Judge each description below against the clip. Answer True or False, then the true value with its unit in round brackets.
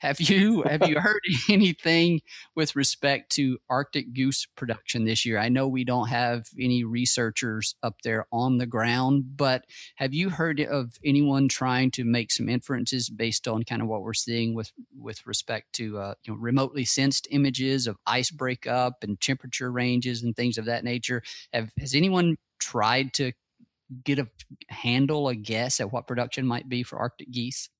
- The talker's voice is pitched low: True (125 Hz)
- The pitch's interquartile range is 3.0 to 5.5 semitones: False (2.6 semitones)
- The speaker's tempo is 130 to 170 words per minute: False (180 wpm)